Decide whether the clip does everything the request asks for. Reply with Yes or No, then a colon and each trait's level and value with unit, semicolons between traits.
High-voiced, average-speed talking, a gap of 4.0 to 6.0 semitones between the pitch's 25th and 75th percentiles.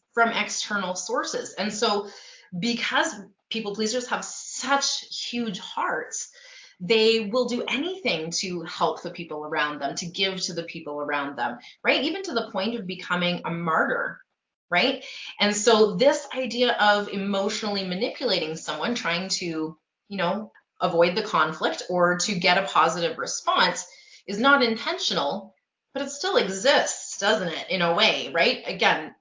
Yes: high, 205 Hz; average, 150 wpm; wide, 5.6 semitones